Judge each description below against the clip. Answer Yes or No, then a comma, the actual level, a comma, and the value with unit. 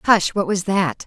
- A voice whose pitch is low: No, medium, 185 Hz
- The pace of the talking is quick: Yes, fast, 225 wpm